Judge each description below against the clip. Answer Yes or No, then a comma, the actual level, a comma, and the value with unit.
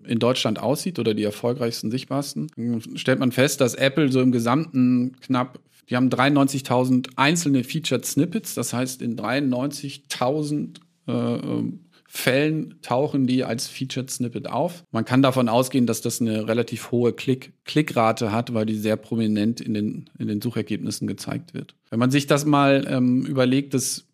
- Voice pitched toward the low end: Yes, low, 125 Hz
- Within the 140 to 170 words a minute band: Yes, average, 160 wpm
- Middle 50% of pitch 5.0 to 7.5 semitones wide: No, average, 2.8 semitones